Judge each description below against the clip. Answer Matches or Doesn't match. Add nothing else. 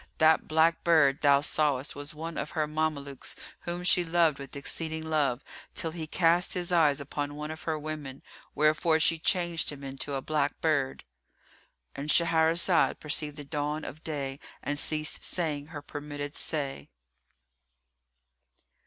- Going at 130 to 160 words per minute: Matches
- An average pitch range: Doesn't match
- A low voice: Doesn't match